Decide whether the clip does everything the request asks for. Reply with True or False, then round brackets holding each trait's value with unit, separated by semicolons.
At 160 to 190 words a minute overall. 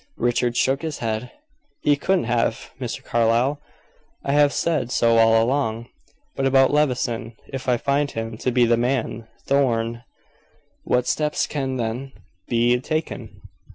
False (145 wpm)